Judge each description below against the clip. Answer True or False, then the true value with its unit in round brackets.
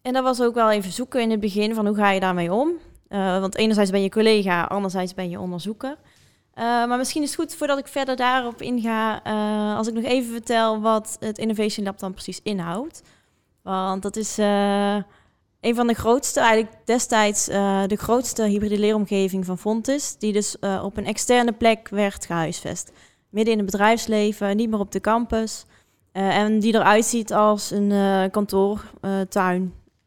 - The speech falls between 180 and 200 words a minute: True (190 wpm)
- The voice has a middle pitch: False (215 Hz)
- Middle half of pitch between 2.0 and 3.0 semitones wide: True (2.6 semitones)